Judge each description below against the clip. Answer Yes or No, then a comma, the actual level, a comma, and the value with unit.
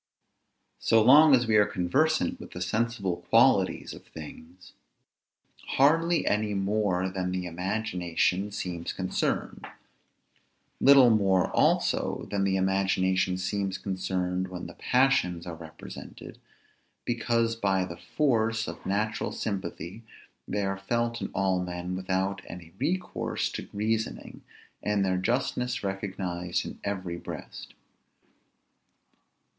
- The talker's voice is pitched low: Yes, very low, 95 Hz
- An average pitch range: Yes, average, 3.8 semitones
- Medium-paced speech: No, slow, 120 wpm